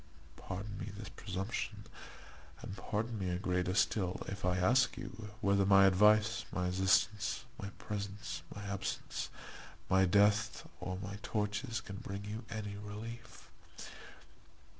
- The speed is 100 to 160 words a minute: Yes, slow, 135 wpm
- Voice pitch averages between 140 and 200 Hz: No, low, 100 Hz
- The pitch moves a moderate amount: No, narrow, 2.1 semitones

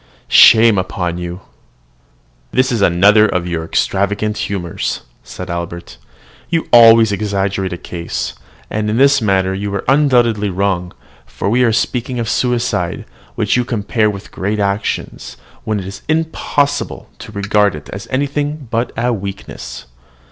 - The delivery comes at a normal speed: Yes, average, 150 wpm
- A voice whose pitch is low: Yes, low, 105 Hz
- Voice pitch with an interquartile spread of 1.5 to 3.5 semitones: No, average, 3.9 semitones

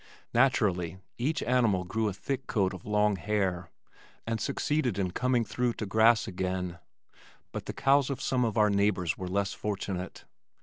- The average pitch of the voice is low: Yes, low, 105 Hz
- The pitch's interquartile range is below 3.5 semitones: No, average, 4.4 semitones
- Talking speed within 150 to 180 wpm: Yes, average, 165 wpm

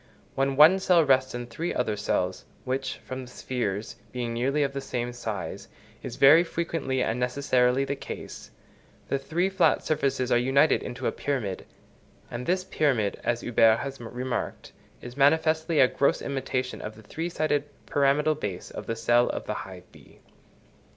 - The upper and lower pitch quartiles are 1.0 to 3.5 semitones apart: Yes, average, 3.2 semitones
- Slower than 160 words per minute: No, average, 170 wpm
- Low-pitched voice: Yes, low, 130 Hz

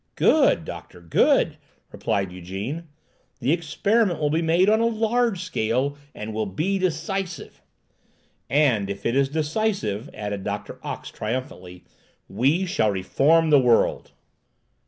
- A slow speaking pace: Yes, slow, 130 wpm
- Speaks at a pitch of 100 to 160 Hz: Yes, medium, 140 Hz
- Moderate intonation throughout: No, wide, 8.9 semitones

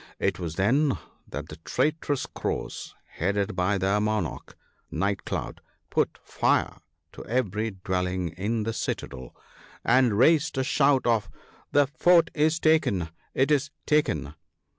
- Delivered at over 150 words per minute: No, average, 140 wpm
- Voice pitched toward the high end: No, low, 110 Hz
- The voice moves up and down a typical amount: No, wide, 7.3 semitones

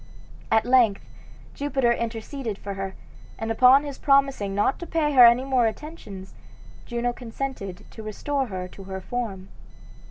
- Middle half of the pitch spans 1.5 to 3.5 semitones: No, average, 5.1 semitones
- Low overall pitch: No, high, 235 Hz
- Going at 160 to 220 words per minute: No, average, 150 wpm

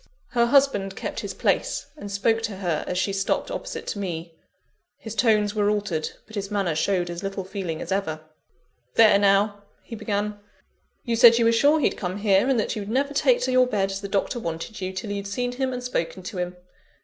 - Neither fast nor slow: No, fast, 215 wpm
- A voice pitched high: Yes, high, 205 Hz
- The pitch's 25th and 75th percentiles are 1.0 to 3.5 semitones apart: Yes, average, 3.1 semitones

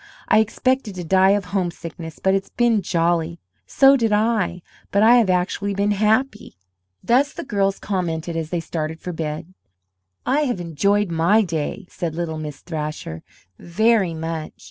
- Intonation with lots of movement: No, average, 4.3 semitones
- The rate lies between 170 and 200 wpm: No, average, 160 wpm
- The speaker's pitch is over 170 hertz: Yes, medium, 185 Hz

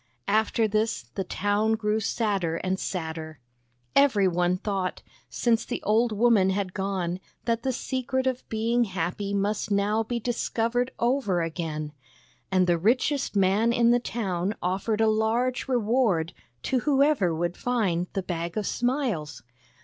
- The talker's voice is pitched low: No, high, 210 Hz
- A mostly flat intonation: No, average, 4.5 semitones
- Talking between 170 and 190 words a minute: No, average, 145 wpm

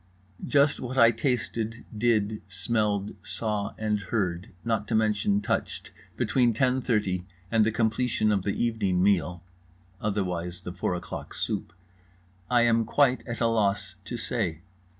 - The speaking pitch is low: Yes, low, 110 Hz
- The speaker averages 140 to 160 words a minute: Yes, average, 145 wpm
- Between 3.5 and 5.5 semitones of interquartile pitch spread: No, average, 2.9 semitones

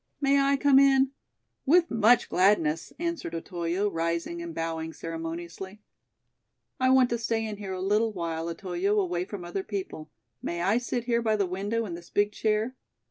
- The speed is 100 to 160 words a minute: No, average, 175 wpm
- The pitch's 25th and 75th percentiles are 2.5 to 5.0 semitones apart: No, wide, 5.6 semitones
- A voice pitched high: Yes, high, 205 Hz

